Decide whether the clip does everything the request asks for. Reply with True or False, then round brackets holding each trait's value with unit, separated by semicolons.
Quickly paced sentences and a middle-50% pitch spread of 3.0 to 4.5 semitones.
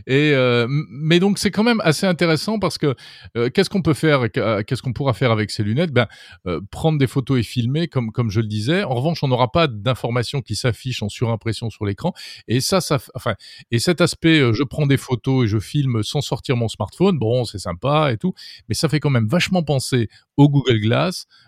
False (225 wpm; 5.2 semitones)